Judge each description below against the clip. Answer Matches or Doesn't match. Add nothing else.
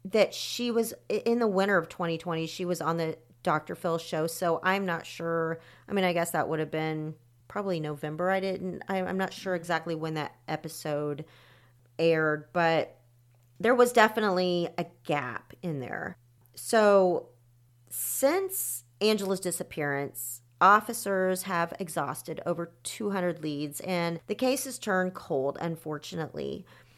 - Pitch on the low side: Doesn't match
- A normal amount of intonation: Matches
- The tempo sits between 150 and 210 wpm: Doesn't match